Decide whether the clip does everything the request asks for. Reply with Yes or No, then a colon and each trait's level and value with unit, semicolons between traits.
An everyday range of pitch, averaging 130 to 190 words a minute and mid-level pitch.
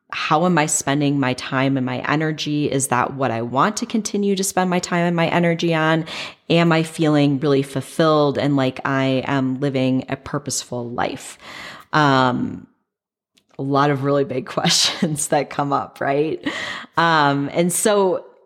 Yes: average, 3.7 semitones; average, 165 wpm; medium, 145 Hz